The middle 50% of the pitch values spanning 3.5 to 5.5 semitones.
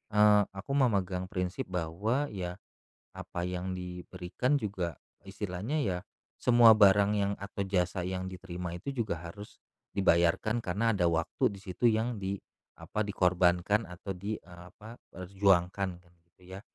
No: average, 2.7 semitones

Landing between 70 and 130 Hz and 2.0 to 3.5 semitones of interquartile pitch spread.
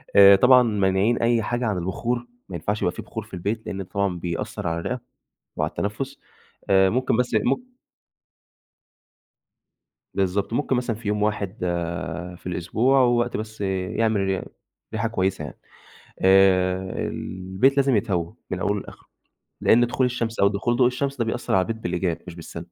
No: low, 105 Hz; average, 4.3 semitones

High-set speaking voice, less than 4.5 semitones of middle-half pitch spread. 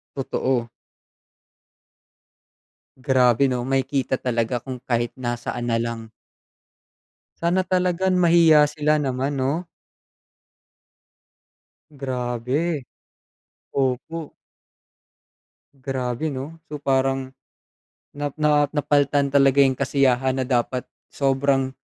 No: low, 135 Hz; narrow, 2.6 semitones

